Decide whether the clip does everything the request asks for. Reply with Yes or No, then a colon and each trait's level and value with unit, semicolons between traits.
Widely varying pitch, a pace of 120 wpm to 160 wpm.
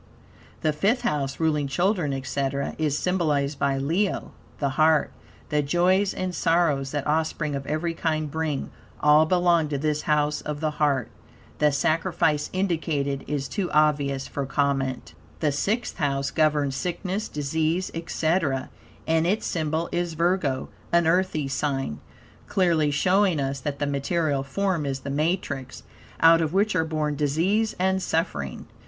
No: average, 3.4 semitones; average, 150 wpm